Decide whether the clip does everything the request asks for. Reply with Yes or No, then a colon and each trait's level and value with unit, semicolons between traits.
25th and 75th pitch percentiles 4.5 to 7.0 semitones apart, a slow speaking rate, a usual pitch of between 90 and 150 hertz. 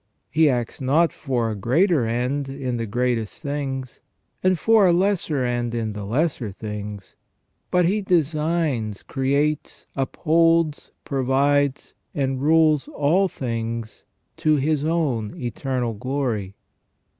Yes: average, 4.8 semitones; slow, 120 wpm; low, 135 Hz